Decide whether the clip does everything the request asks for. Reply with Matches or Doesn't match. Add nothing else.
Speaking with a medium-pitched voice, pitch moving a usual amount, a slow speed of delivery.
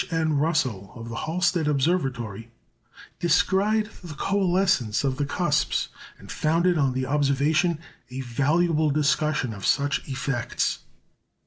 Matches